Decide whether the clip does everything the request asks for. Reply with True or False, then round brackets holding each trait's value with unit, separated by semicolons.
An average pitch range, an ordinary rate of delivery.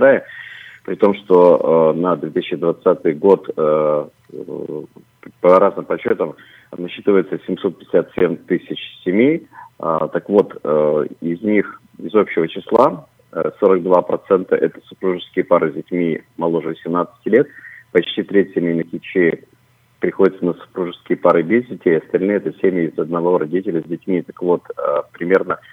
False (2.1 semitones; 130 wpm)